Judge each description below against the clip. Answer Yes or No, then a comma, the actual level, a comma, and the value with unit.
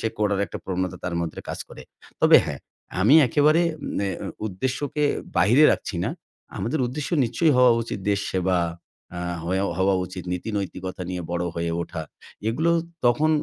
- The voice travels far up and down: Yes, wide, 5.7 semitones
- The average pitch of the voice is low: Yes, low, 100 Hz